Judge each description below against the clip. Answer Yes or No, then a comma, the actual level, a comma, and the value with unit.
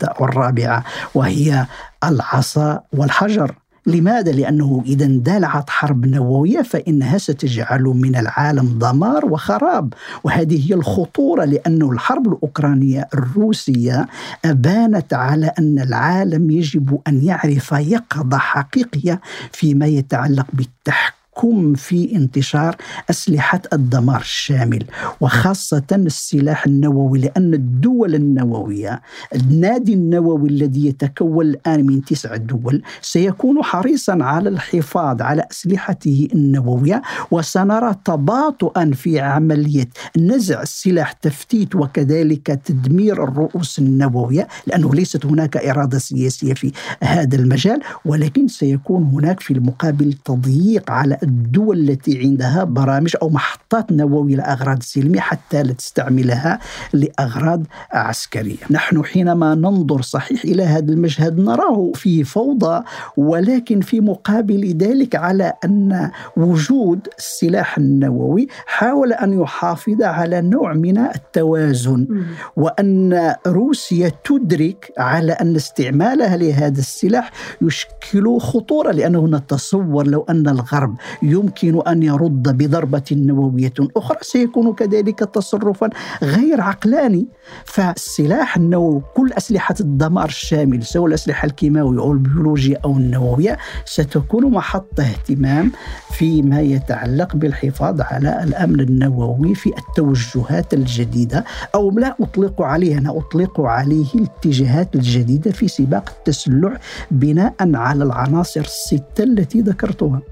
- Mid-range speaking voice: Yes, medium, 155 Hz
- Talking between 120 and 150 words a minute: No, average, 105 wpm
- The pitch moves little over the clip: No, average, 5.2 semitones